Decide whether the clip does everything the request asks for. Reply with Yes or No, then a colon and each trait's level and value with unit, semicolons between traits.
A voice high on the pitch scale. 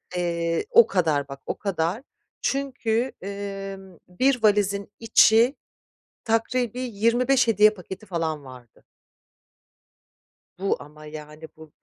Yes: high, 200 Hz